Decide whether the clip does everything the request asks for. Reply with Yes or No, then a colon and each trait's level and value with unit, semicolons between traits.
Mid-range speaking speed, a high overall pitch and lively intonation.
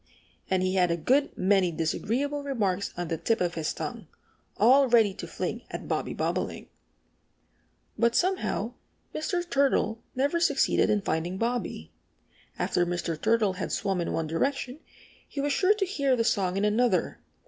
Yes: average, 160 wpm; high, 215 Hz; wide, 7.1 semitones